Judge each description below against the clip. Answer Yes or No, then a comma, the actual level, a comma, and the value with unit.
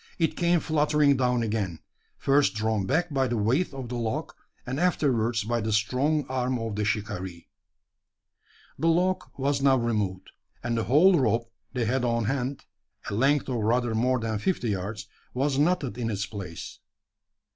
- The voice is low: Yes, low, 120 Hz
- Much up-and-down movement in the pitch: No, average, 4.2 semitones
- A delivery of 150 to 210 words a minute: Yes, average, 165 wpm